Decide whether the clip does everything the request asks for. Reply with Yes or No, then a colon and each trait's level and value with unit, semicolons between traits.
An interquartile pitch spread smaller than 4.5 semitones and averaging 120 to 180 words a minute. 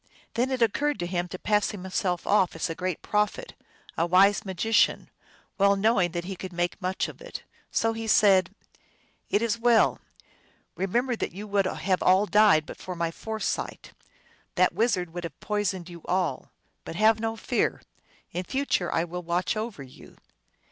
Yes: average, 3.8 semitones; average, 175 wpm